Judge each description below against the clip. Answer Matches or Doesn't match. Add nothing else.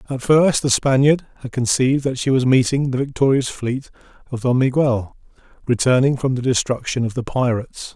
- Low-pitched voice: Matches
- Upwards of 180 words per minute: Doesn't match